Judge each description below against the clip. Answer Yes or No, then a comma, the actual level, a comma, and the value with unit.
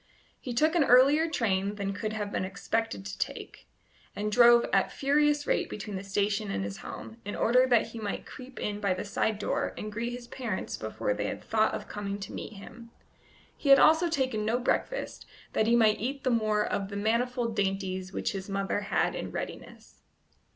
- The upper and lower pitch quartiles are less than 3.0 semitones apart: No, average, 3.7 semitones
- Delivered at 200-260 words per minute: Yes, fast, 205 wpm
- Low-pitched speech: No, high, 215 Hz